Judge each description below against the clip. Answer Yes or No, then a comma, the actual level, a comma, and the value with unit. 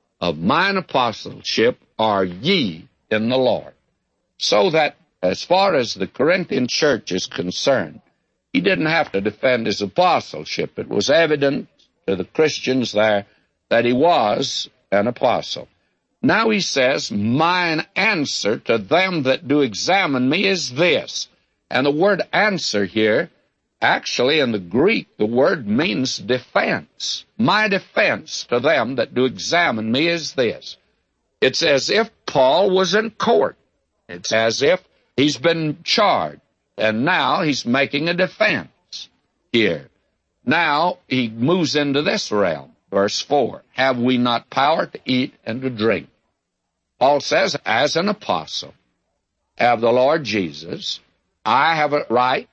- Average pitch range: No, wide, 6.8 semitones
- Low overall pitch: Yes, low, 130 Hz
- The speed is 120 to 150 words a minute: Yes, average, 140 wpm